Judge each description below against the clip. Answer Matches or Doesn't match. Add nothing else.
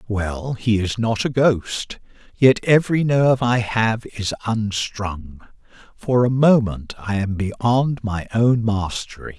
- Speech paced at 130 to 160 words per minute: Matches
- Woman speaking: Doesn't match